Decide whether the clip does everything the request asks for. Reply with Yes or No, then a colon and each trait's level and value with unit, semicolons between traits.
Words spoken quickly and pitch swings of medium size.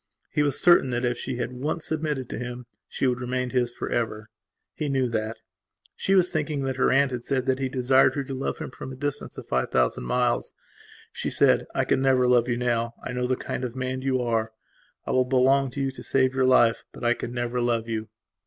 No: fast, 235 wpm; narrow, 1.9 semitones